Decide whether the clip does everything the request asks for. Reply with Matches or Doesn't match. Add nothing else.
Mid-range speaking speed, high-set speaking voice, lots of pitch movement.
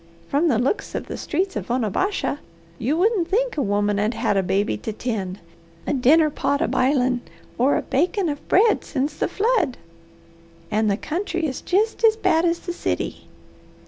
Matches